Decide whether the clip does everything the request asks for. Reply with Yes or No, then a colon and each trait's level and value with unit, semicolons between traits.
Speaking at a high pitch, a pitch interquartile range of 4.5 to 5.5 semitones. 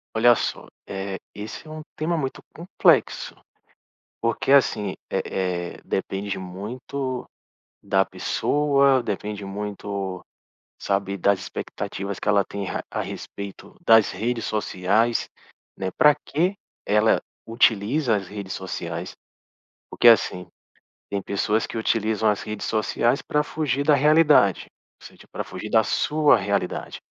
No: low, 105 Hz; average, 4.9 semitones